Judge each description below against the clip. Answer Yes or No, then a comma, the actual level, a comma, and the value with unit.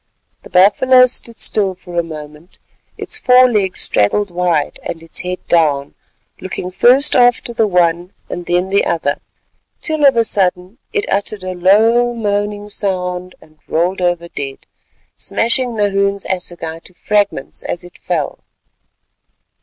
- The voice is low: No, medium, 185 Hz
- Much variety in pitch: No, average, 3.6 semitones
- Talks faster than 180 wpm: No, average, 145 wpm